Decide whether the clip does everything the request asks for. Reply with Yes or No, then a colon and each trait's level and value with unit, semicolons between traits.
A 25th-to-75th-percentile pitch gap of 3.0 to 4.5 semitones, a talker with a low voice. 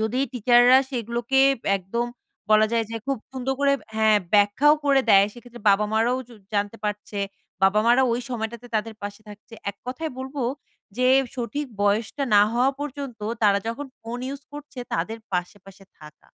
No: average, 4.1 semitones; high, 235 Hz